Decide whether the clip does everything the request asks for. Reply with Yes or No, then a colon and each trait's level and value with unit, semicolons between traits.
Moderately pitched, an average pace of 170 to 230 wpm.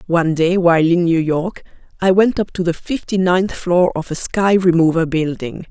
Yes: medium, 175 Hz; average, 200 wpm